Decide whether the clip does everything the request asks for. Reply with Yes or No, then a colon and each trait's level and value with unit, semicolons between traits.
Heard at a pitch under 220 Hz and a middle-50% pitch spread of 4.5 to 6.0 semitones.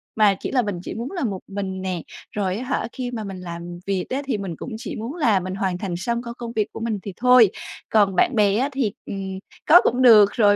No: high, 210 Hz; average, 4.1 semitones